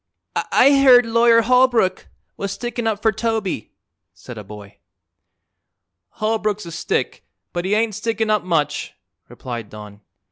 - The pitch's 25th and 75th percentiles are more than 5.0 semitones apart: Yes, wide, 5.4 semitones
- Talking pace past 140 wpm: No, slow, 135 wpm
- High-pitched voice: Yes, high, 215 Hz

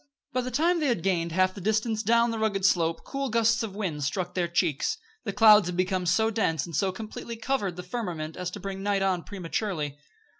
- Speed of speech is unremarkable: No, fast, 220 wpm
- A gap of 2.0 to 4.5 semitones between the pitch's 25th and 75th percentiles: Yes, average, 4.0 semitones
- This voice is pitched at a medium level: No, high, 195 Hz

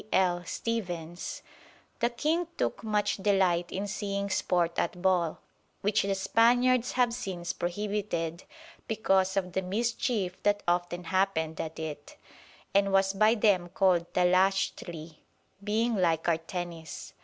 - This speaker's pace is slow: Yes, slow, 130 wpm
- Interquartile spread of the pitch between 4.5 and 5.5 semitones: No, average, 3.1 semitones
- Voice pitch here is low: No, high, 190 Hz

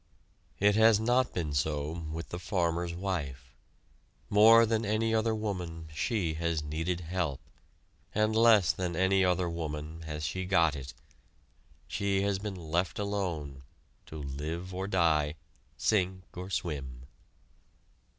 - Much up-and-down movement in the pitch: No, average, 4.4 semitones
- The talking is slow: Yes, slow, 130 wpm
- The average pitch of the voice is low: Yes, very low, 90 Hz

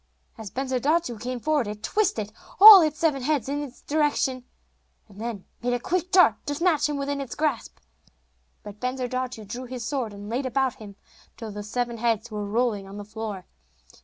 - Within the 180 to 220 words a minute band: Yes, average, 185 wpm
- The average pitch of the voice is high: Yes, very high, 250 Hz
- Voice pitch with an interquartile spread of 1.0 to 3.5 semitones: No, average, 4.9 semitones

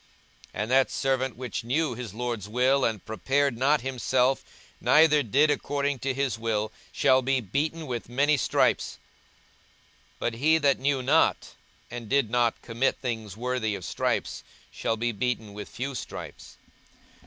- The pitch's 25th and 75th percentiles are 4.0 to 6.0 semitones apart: No, average, 3.2 semitones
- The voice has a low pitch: Yes, low, 125 Hz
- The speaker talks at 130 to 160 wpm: Yes, average, 155 wpm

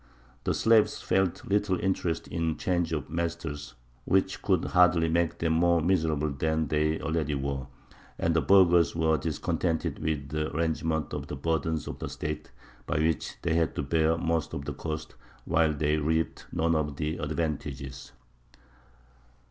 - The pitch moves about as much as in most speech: No, narrow, 1.6 semitones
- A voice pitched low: Yes, very low, 80 Hz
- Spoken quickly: No, average, 160 wpm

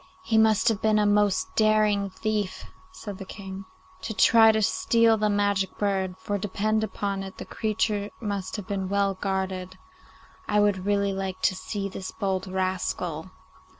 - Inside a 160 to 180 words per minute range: Yes, average, 165 wpm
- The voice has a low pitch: No, high, 200 Hz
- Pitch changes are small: Yes, narrow, 2.0 semitones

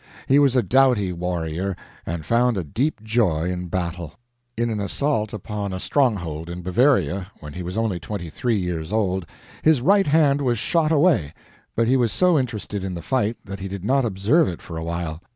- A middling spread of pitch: No, wide, 6.3 semitones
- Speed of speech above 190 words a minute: Yes, average, 200 wpm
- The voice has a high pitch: No, low, 100 Hz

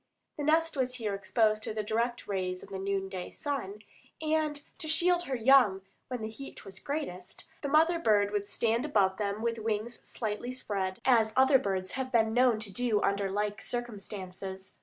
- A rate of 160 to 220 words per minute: Yes, average, 185 wpm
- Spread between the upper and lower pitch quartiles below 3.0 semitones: No, average, 4.8 semitones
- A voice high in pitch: Yes, high, 220 Hz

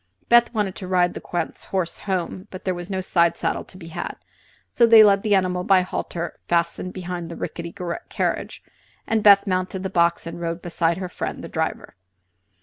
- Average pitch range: No, narrow, 2.2 semitones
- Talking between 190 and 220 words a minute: Yes, average, 200 wpm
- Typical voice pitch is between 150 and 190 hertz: Yes, medium, 185 Hz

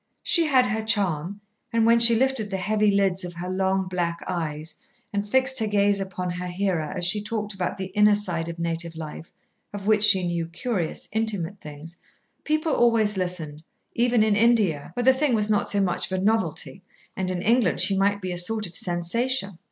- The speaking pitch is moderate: No, high, 195 Hz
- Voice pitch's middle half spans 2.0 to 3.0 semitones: No, average, 3.8 semitones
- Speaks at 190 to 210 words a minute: Yes, fast, 205 wpm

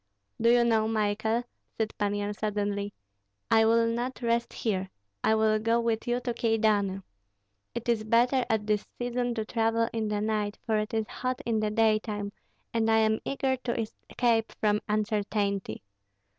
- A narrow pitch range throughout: Yes, narrow, 1.8 semitones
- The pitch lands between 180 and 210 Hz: No, high, 220 Hz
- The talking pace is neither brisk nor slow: Yes, average, 170 wpm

